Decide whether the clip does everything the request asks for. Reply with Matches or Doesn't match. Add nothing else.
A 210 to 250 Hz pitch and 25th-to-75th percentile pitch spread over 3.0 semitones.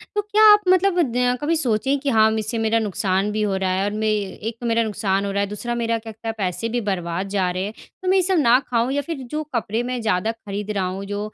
Matches